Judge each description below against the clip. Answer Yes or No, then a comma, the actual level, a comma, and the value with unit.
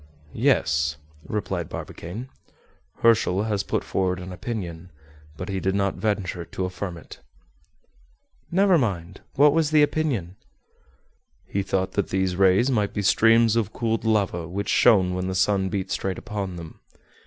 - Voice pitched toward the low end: Yes, very low, 95 Hz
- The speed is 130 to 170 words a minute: Yes, average, 150 wpm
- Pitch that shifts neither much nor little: Yes, average, 3.4 semitones